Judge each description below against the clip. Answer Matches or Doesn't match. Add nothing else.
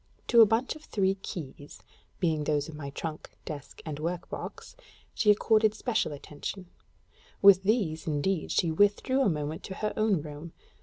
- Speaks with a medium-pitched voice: Matches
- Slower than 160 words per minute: Doesn't match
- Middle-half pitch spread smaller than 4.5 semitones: Doesn't match